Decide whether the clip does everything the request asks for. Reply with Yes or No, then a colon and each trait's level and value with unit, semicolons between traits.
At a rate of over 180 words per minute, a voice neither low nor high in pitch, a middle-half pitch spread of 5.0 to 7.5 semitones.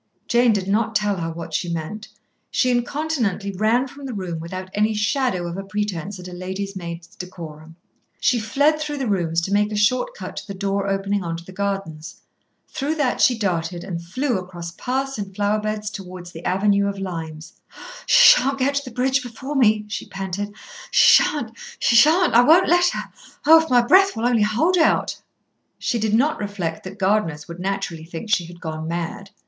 No: average, 195 wpm; high, 205 Hz; wide, 5.4 semitones